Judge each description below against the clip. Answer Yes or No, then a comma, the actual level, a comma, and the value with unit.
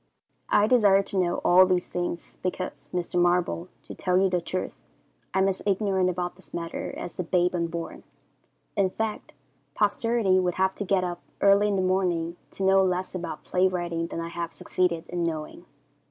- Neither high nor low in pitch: Yes, medium, 180 Hz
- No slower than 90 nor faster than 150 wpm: No, average, 185 wpm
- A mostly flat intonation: Yes, narrow, 1.7 semitones